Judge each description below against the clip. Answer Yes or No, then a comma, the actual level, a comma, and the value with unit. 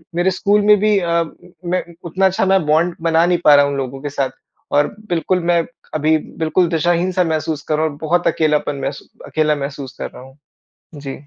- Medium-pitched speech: Yes, medium, 160 Hz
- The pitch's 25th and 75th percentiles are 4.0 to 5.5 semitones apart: No, average, 3.1 semitones